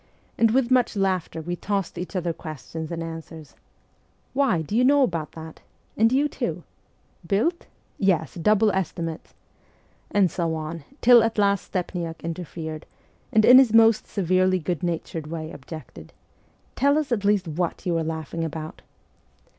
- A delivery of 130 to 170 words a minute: No, average, 180 wpm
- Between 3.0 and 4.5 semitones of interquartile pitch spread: No, average, 4.9 semitones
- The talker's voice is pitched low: No, medium, 180 Hz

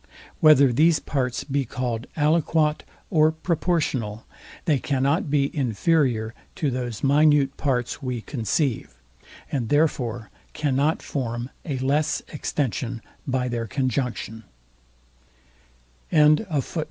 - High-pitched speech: No, low, 135 Hz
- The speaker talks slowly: Yes, slow, 100 wpm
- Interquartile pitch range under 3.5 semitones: No, average, 3.8 semitones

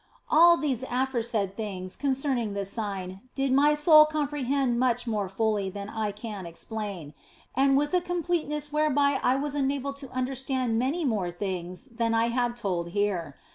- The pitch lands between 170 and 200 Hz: No, high, 245 Hz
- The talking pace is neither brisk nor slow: Yes, average, 165 wpm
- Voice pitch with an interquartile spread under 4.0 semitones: No, wide, 5.6 semitones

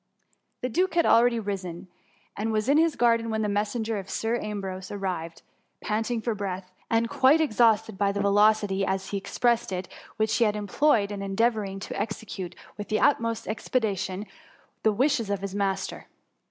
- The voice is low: No, high, 215 Hz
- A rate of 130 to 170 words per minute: No, average, 185 wpm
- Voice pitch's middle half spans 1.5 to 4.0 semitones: Yes, average, 2.7 semitones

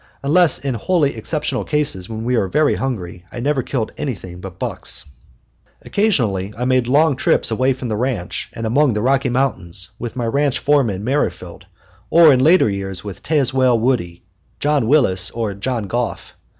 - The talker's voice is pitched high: No, low, 125 Hz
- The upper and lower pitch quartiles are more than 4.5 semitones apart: Yes, wide, 5.6 semitones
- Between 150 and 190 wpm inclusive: Yes, average, 170 wpm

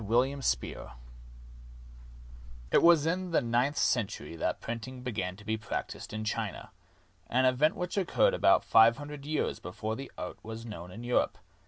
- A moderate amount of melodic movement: Yes, average, 4.9 semitones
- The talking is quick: No, average, 165 wpm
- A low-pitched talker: Yes, low, 120 Hz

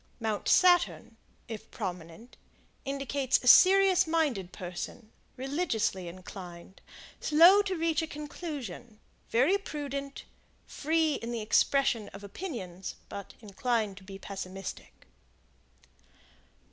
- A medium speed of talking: No, slow, 105 wpm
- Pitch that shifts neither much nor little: No, wide, 7.9 semitones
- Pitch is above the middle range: Yes, high, 245 Hz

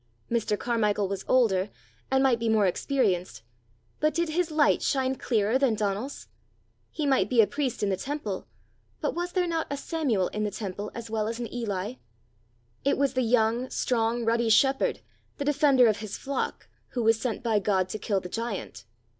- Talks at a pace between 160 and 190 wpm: Yes, average, 185 wpm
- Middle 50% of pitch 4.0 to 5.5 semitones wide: Yes, average, 4.4 semitones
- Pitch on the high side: Yes, high, 230 Hz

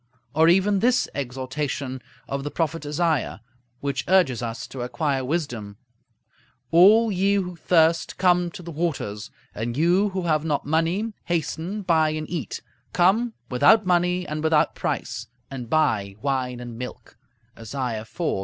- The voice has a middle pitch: Yes, medium, 155 Hz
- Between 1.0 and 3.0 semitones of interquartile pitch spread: No, average, 5.3 semitones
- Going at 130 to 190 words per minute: Yes, average, 145 wpm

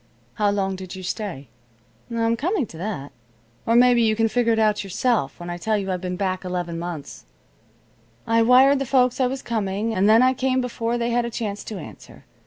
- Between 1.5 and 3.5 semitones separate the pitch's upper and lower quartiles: No, average, 4.3 semitones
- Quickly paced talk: Yes, fast, 210 wpm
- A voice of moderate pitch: No, high, 220 Hz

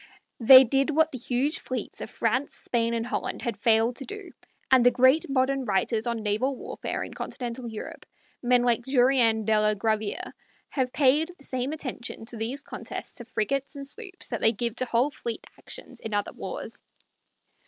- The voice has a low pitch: No, high, 245 Hz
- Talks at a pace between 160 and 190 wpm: Yes, average, 185 wpm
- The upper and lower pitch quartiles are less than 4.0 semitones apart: Yes, average, 3.2 semitones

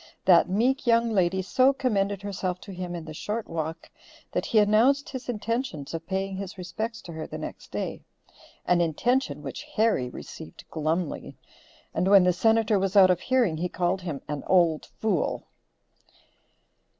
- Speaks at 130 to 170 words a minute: Yes, average, 165 wpm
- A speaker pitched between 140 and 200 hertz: Yes, high, 190 Hz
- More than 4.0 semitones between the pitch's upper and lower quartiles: Yes, average, 4.5 semitones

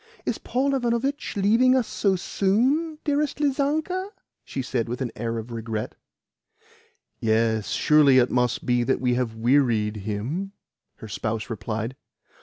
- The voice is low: Yes, low, 130 Hz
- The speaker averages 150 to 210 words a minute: No, average, 140 wpm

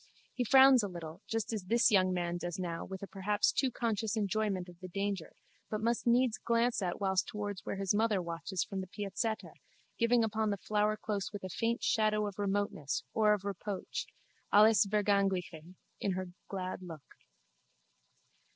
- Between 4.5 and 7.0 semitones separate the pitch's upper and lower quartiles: No, average, 2.8 semitones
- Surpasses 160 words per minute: Yes, average, 170 wpm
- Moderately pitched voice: No, high, 205 Hz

